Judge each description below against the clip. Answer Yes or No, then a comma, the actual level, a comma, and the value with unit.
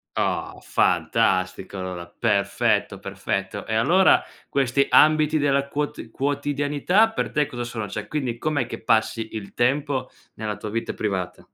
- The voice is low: Yes, low, 120 Hz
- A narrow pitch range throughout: No, wide, 5.8 semitones